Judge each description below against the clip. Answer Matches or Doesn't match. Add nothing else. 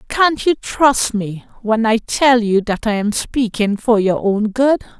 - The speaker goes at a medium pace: Matches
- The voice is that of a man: Doesn't match